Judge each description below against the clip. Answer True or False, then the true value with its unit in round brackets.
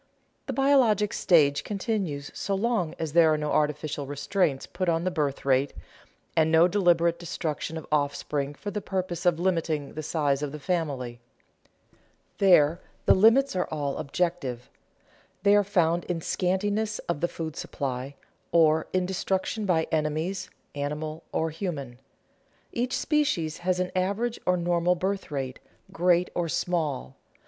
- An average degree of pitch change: True (3.9 semitones)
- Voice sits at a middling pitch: True (170 Hz)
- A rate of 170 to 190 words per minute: False (150 wpm)